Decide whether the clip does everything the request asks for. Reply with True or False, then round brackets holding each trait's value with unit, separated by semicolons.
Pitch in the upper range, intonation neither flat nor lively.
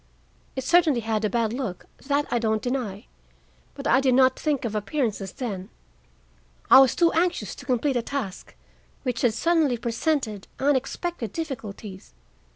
True (250 Hz; 4.4 semitones)